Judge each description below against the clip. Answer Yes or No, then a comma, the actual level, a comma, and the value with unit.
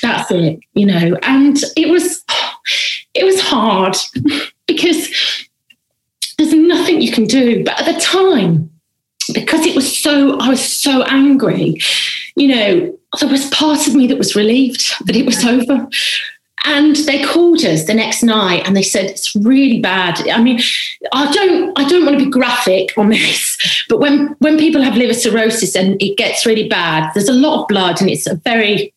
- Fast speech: No, average, 180 wpm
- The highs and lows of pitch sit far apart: Yes, wide, 6.1 semitones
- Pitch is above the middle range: Yes, very high, 265 Hz